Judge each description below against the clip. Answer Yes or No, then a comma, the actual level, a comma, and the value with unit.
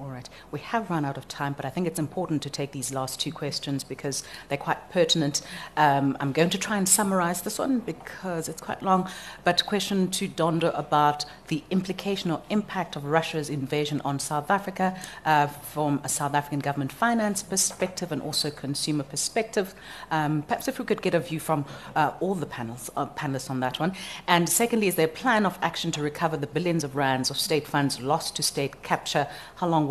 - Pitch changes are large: No, average, 4.4 semitones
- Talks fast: Yes, fast, 210 wpm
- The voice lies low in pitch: No, medium, 160 Hz